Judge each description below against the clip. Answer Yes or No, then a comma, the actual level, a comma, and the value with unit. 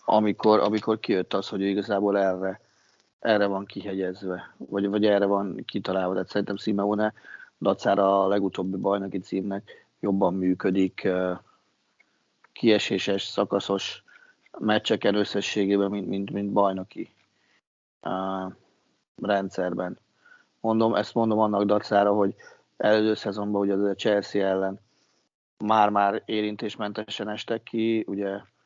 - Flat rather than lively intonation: Yes, narrow, 1.5 semitones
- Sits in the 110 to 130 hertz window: No, low, 100 Hz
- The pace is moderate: Yes, average, 115 wpm